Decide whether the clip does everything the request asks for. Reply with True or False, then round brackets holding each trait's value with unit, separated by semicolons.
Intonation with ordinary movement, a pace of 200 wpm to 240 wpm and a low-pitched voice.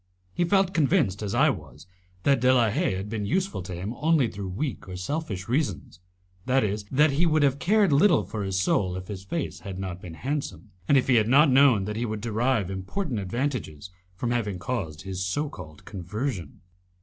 False (6.7 semitones; 205 wpm; 110 Hz)